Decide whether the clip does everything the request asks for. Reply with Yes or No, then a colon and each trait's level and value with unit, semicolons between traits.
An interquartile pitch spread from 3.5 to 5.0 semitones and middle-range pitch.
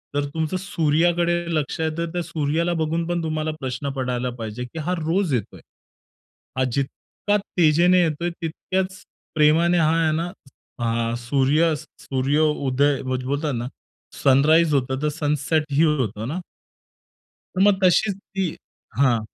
Yes: average, 3.8 semitones; medium, 155 Hz